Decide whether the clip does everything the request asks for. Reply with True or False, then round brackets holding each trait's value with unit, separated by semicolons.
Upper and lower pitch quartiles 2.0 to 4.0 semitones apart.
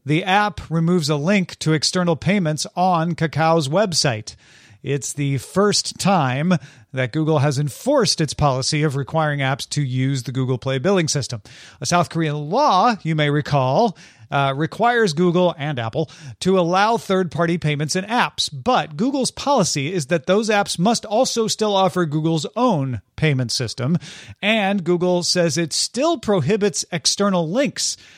False (5.3 semitones)